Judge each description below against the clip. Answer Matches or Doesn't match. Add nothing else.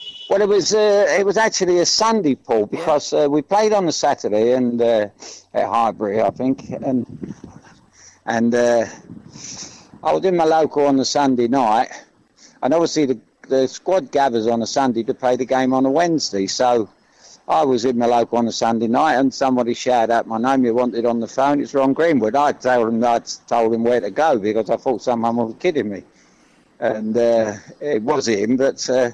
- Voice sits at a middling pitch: Doesn't match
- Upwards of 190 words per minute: Matches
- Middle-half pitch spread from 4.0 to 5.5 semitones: Doesn't match